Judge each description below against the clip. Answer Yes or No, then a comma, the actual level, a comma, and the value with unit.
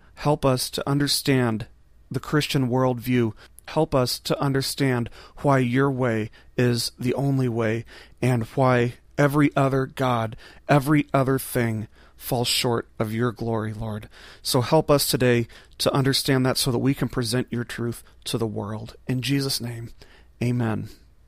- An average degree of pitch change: Yes, average, 3.0 semitones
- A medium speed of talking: Yes, average, 150 wpm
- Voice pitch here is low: Yes, low, 125 Hz